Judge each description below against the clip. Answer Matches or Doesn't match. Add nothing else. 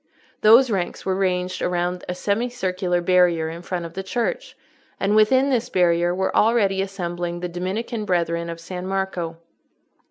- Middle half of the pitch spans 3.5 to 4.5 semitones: Doesn't match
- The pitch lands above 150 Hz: Matches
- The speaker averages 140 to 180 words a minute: Matches